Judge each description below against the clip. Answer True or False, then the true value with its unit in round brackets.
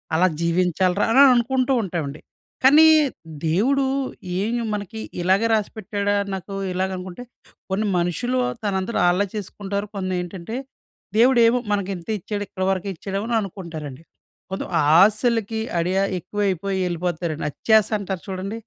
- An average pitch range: True (3.4 semitones)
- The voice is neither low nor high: False (195 Hz)